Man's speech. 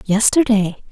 No: female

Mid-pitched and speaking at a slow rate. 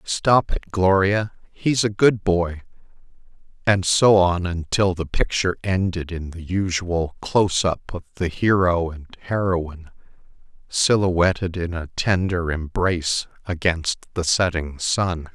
No: very low, 90 Hz; slow, 125 wpm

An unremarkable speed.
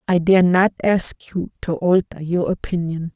Yes: average, 170 wpm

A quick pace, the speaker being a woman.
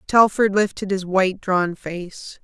No: average, 150 wpm; female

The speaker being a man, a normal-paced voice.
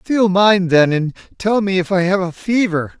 No: male; fast, 220 wpm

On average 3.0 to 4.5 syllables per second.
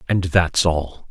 Yes: 3.2 syllables/s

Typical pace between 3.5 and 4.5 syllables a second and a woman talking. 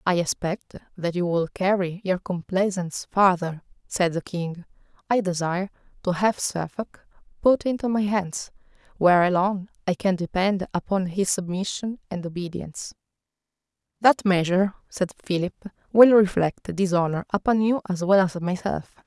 No: 4.9 syllables/s; female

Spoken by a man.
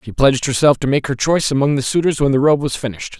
Yes: male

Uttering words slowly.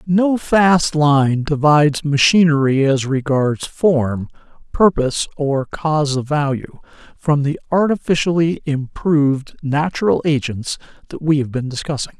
Yes: slow, 120 wpm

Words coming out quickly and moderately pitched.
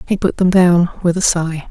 Yes: fast, 245 wpm; medium, 175 Hz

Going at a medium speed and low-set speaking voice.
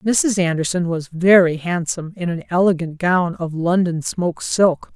No: average, 155 wpm; medium, 175 Hz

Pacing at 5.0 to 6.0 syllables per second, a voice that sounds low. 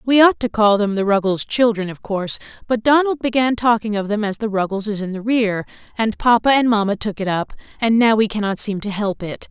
No: 5.6 syllables/s; high, 215 Hz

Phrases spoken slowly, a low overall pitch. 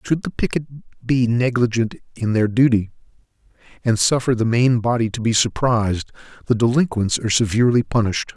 No: average, 160 wpm; low, 120 Hz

